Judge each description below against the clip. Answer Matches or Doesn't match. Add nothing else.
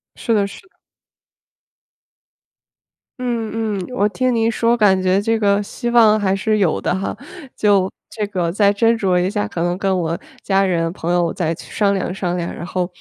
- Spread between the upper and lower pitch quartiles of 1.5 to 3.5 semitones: Matches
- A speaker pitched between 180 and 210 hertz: Matches